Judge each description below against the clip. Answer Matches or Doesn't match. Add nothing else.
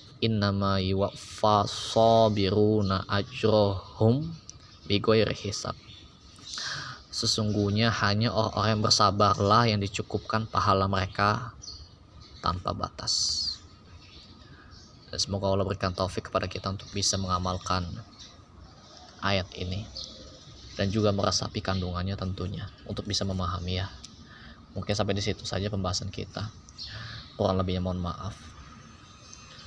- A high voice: Doesn't match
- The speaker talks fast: Doesn't match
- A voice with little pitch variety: Matches